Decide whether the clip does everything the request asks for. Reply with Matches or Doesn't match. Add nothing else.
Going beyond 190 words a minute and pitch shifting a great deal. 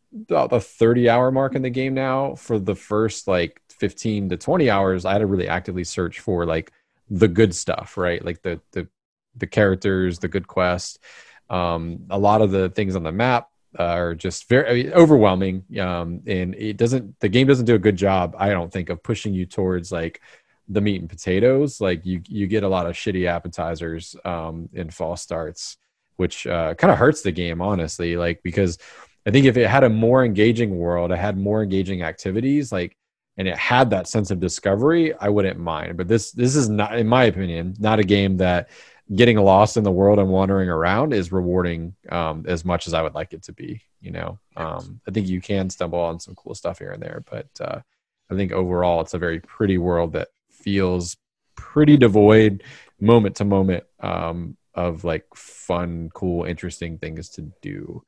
Doesn't match